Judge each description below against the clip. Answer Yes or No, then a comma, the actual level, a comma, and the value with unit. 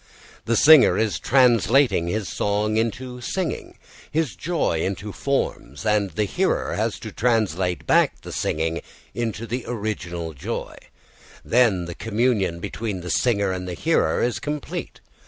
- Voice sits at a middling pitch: No, low, 110 Hz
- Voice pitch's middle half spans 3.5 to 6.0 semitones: Yes, average, 5.1 semitones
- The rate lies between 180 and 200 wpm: No, average, 140 wpm